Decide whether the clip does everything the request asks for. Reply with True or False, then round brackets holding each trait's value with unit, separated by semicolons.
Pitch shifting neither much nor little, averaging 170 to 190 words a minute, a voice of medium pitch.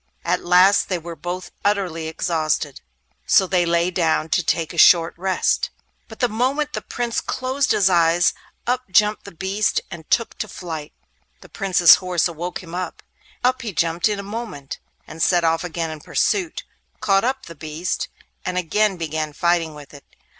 True (3.8 semitones; 175 wpm; 180 Hz)